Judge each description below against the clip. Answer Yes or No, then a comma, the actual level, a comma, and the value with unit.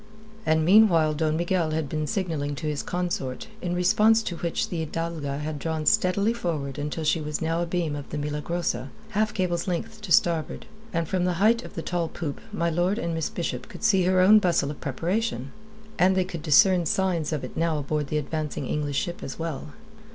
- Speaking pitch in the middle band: Yes, medium, 165 Hz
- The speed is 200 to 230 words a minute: Yes, fast, 205 wpm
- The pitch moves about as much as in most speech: Yes, average, 3.3 semitones